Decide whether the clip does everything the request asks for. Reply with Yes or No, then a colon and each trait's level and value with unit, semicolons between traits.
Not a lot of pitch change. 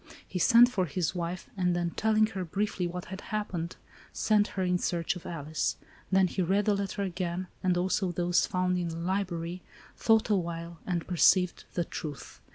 Yes: narrow, 2.1 semitones